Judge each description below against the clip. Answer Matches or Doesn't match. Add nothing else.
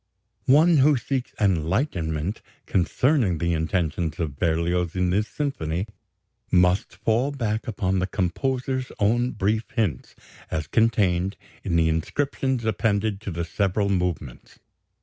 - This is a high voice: Doesn't match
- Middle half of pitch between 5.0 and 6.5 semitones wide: Matches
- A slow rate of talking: Matches